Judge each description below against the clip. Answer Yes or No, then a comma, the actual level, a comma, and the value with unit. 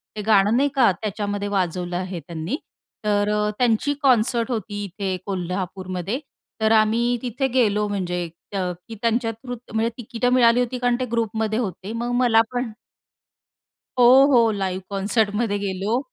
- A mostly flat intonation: No, average, 3.4 semitones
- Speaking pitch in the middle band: No, high, 215 Hz